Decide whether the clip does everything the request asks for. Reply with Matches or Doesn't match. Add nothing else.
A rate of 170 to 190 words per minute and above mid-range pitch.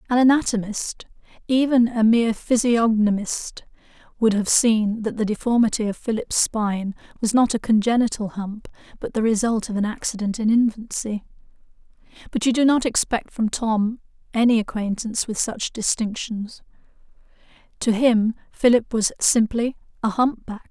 Doesn't match